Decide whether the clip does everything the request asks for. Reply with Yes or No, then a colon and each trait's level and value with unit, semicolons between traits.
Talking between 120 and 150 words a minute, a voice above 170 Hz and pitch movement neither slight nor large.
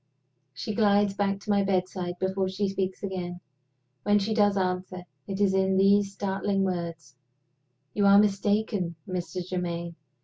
No: average, 145 wpm; high, 190 Hz; narrow, 1.8 semitones